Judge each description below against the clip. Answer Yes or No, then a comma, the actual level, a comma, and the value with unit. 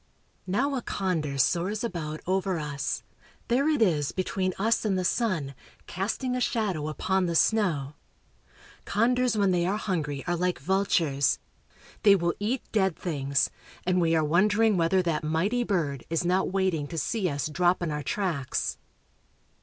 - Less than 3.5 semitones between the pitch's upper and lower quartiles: No, average, 4.9 semitones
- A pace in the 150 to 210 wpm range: Yes, average, 160 wpm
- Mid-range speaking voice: Yes, medium, 180 Hz